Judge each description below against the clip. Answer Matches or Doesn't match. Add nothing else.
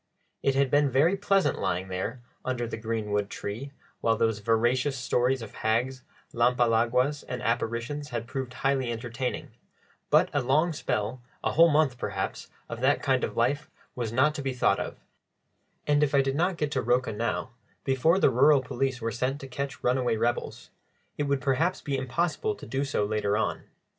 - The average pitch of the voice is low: Matches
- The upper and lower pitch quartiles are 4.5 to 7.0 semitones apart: Doesn't match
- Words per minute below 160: Doesn't match